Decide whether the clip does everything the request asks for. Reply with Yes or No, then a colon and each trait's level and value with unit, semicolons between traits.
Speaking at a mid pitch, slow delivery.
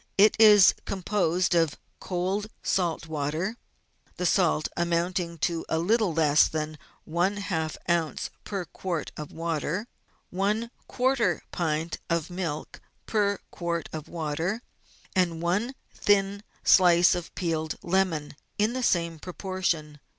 Yes: medium, 175 Hz; slow, 125 wpm